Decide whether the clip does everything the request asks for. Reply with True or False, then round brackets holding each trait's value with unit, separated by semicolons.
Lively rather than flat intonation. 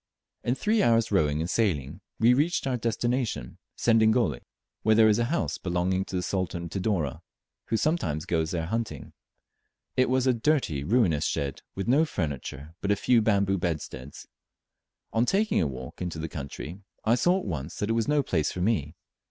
True (6.9 semitones)